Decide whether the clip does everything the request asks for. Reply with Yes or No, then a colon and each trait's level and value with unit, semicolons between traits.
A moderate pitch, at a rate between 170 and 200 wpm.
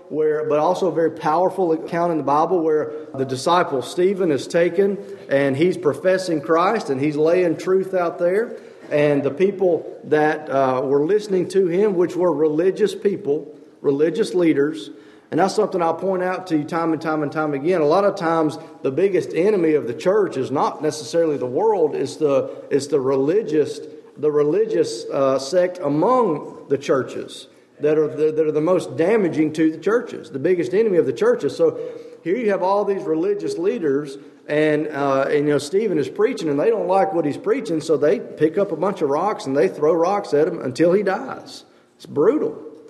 Yes: medium, 175 Hz; average, 195 wpm